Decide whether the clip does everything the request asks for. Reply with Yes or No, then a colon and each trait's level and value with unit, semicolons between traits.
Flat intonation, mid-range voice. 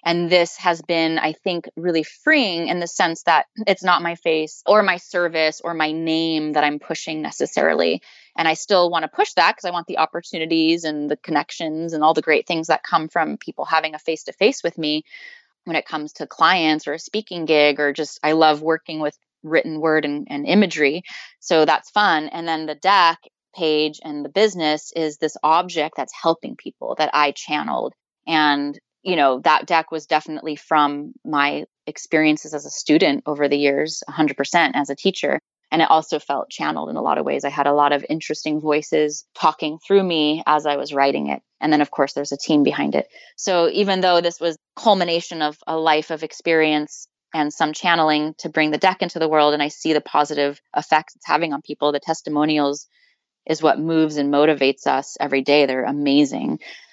Yes: narrow, 2.1 semitones; medium, 155 Hz